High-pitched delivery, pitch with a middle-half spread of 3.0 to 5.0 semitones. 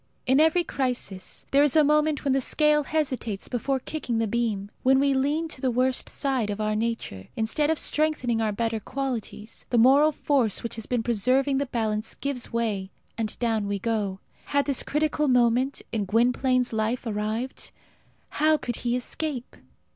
Yes: very high, 250 Hz; average, 3.9 semitones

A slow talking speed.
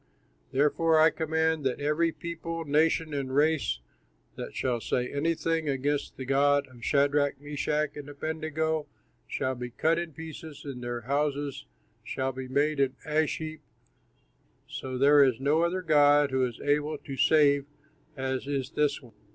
No: average, 160 wpm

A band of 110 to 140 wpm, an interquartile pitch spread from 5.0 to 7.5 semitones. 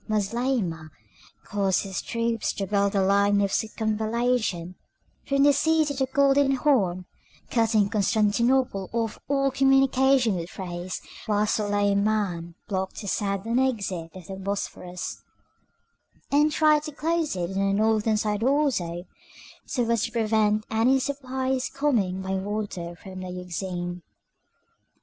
Yes: slow, 135 wpm; average, 5.3 semitones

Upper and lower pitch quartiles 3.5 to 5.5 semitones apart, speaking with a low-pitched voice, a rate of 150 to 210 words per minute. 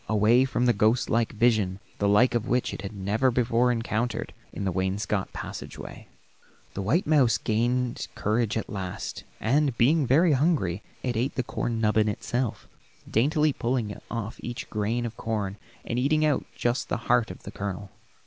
No: average, 3.1 semitones; low, 115 Hz; average, 170 wpm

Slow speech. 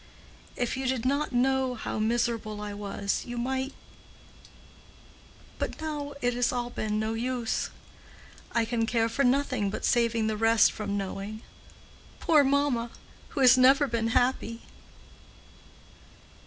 Yes: slow, 130 wpm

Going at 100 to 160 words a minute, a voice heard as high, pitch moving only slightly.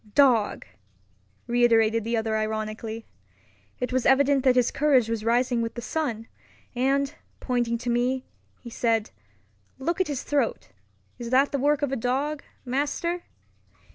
No: average, 145 wpm; very high, 250 Hz; average, 3.4 semitones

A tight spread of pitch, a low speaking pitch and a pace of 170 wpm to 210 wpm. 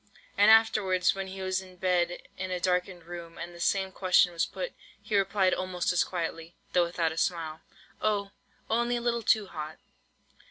No: narrow, 2.3 semitones; medium, 185 Hz; average, 175 wpm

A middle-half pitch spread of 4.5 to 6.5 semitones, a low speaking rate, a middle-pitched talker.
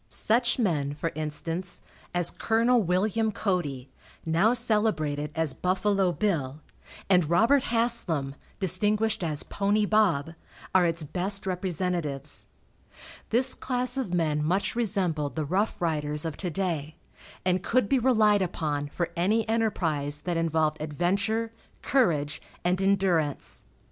Yes: wide, 5.4 semitones; slow, 125 wpm; medium, 180 Hz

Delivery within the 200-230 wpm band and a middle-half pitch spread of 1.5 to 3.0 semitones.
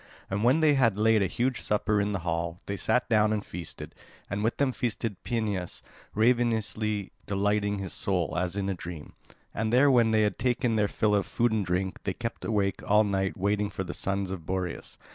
Yes: fast, 205 wpm; narrow, 2.6 semitones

